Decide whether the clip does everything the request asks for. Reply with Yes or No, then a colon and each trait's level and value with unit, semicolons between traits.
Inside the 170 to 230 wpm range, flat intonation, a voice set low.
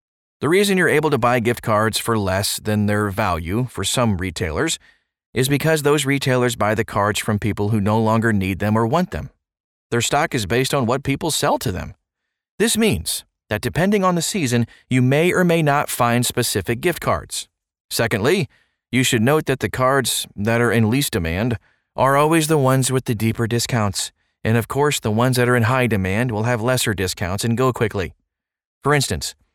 No: average, 200 wpm; average, 4.5 semitones; low, 120 Hz